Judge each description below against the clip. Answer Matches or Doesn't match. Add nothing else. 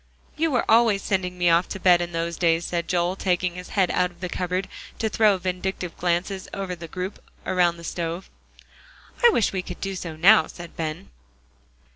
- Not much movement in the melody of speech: Matches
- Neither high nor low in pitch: Matches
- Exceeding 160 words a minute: Matches